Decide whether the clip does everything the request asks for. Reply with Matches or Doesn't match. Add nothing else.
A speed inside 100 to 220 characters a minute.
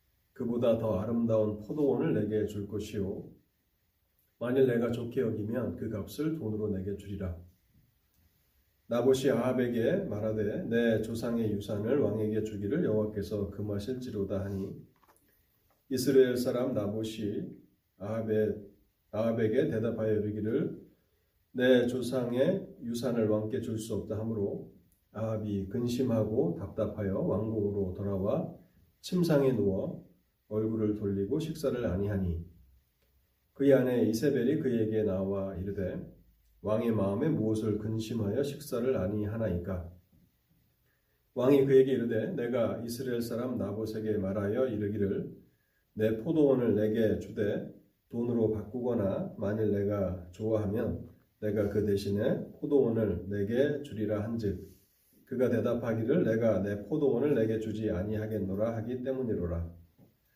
Doesn't match